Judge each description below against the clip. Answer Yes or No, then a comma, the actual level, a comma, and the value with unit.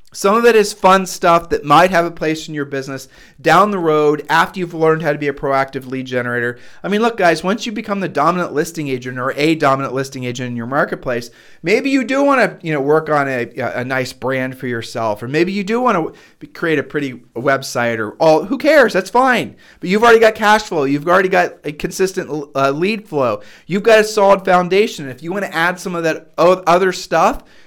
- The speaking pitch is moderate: Yes, medium, 160 Hz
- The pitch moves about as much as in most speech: No, wide, 6.0 semitones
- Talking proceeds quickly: Yes, fast, 230 wpm